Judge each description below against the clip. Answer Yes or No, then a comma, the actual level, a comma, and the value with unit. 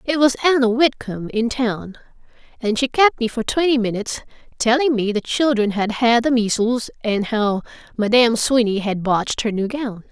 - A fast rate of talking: No, average, 180 wpm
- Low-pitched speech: No, high, 235 Hz